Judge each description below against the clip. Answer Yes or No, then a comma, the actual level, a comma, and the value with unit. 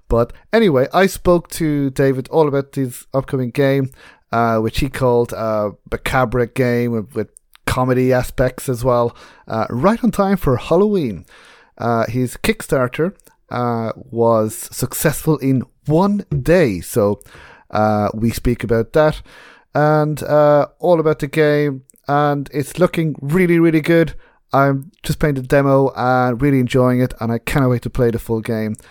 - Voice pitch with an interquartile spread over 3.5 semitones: Yes, average, 4.2 semitones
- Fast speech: No, average, 160 wpm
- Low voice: Yes, low, 130 Hz